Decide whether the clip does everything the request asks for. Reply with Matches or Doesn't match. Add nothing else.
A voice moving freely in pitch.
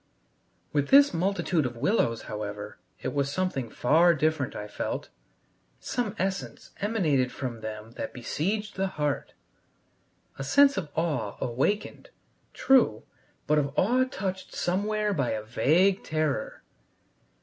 Matches